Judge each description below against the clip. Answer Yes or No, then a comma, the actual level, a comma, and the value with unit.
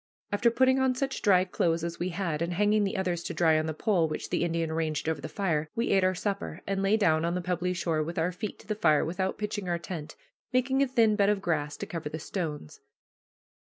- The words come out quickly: Yes, fast, 245 wpm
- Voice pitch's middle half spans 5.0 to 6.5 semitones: No, average, 4.2 semitones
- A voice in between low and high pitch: Yes, medium, 180 Hz